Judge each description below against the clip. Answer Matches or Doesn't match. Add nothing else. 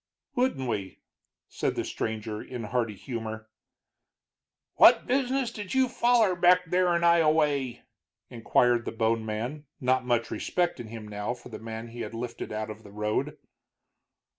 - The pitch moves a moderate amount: Doesn't match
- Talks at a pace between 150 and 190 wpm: Matches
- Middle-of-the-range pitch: Doesn't match